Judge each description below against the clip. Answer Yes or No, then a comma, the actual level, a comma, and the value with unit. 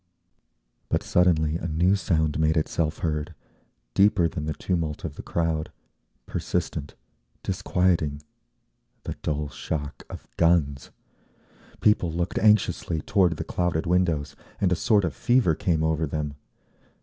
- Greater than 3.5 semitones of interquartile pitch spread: No, average, 2.8 semitones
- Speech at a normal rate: No, slow, 125 wpm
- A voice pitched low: Yes, very low, 80 Hz